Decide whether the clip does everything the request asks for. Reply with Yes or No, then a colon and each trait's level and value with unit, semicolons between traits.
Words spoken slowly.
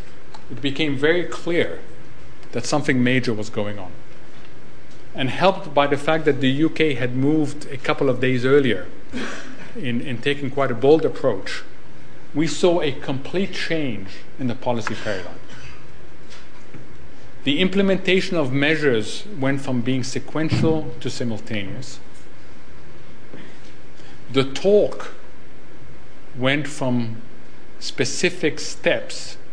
Yes: slow, 115 wpm